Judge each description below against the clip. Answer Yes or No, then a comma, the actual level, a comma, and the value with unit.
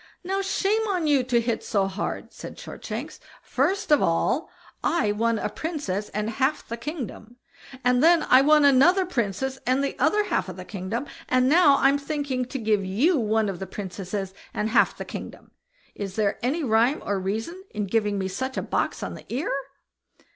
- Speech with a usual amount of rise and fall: No, wide, 6.2 semitones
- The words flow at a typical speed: Yes, average, 190 wpm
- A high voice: Yes, very high, 250 Hz